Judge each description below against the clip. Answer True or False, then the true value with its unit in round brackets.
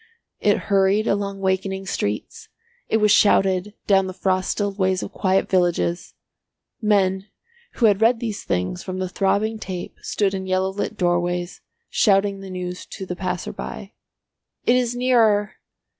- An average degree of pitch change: False (2.0 semitones)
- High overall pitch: True (195 Hz)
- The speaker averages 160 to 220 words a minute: False (150 wpm)